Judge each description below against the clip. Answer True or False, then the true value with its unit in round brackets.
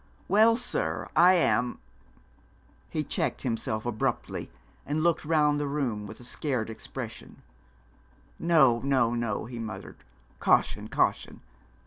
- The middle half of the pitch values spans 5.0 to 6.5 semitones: True (5.3 semitones)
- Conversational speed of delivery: False (125 wpm)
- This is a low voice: True (130 Hz)